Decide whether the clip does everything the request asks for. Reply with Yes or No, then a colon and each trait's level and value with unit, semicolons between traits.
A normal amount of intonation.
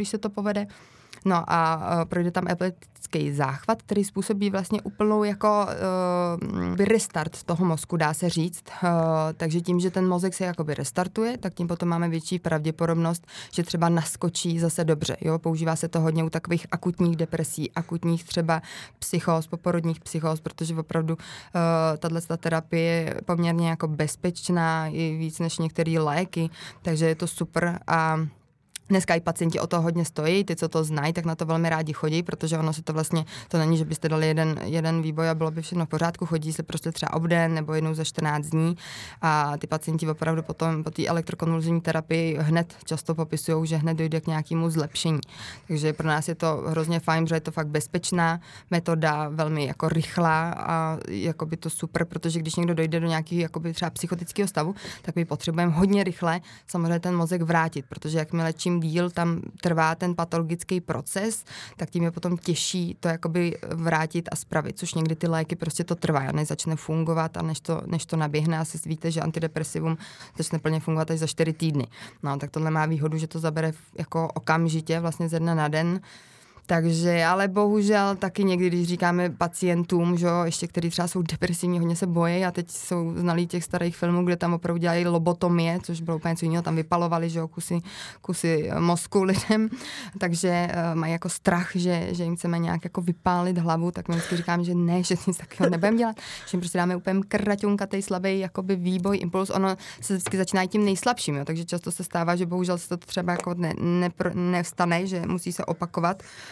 No: narrow, 1.6 semitones